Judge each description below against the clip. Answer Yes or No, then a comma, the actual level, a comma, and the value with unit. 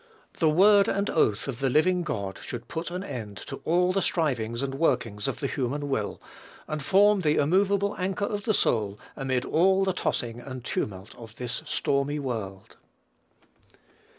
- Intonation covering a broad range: Yes, wide, 7.5 semitones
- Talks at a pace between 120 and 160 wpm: No, average, 170 wpm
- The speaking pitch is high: No, medium, 145 Hz